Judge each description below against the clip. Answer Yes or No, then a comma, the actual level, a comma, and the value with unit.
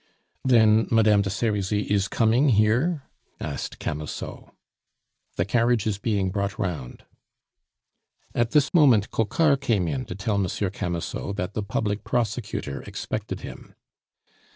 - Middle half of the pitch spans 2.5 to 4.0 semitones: Yes, average, 3.1 semitones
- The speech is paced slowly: Yes, slow, 130 wpm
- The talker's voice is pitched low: Yes, low, 105 Hz